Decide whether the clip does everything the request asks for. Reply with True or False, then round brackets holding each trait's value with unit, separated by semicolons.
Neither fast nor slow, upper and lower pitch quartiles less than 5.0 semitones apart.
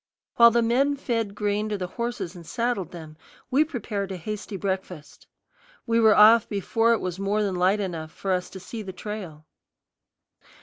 True (180 wpm; 3.8 semitones)